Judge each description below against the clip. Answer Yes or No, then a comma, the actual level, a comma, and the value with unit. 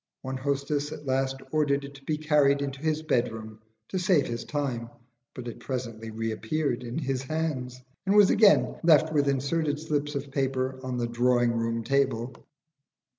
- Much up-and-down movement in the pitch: No, average, 3.3 semitones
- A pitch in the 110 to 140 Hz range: Yes, low, 135 Hz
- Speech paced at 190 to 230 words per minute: No, average, 170 wpm